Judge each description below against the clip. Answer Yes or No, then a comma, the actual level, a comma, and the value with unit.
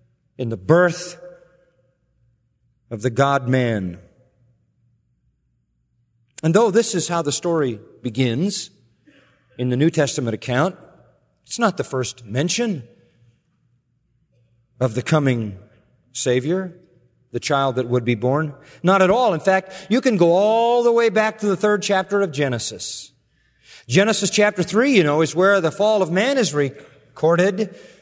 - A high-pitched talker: No, medium, 140 Hz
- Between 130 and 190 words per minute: Yes, average, 140 wpm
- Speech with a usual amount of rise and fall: No, wide, 7.4 semitones